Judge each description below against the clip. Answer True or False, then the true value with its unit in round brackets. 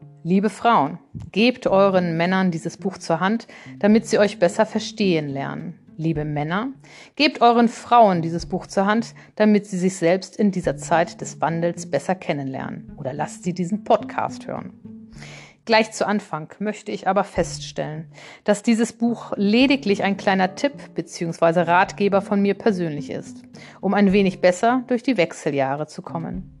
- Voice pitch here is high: True (195 Hz)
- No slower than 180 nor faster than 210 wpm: False (160 wpm)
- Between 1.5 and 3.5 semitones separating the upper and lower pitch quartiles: False (4.3 semitones)